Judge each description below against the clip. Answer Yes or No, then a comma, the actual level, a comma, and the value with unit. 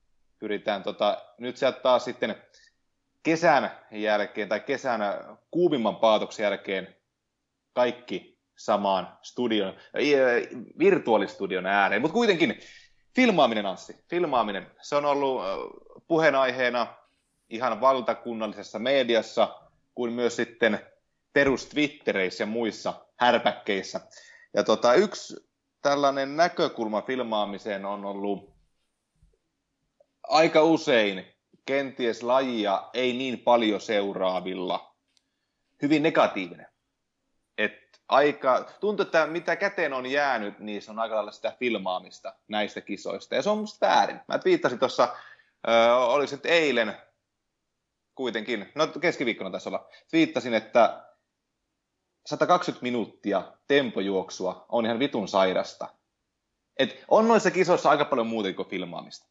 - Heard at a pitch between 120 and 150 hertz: Yes, low, 125 Hz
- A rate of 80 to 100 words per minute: No, average, 110 wpm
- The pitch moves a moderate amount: No, wide, 6.4 semitones